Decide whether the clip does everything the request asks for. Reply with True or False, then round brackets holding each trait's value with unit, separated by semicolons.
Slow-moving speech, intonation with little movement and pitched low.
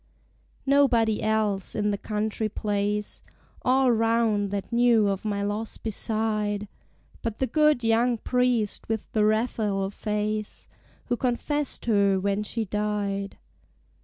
False (125 wpm; 2.2 semitones; 215 Hz)